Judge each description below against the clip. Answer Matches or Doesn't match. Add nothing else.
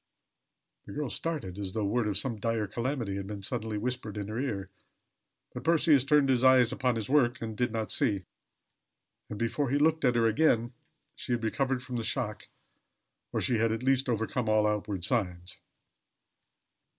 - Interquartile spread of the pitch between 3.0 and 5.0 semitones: Matches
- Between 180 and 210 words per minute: Matches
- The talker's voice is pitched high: Doesn't match